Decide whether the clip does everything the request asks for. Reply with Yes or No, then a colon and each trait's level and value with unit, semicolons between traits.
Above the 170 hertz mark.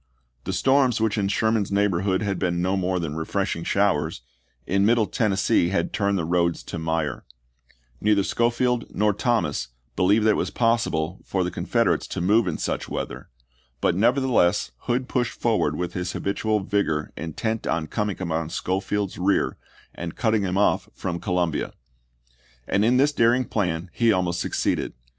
No: low, 100 Hz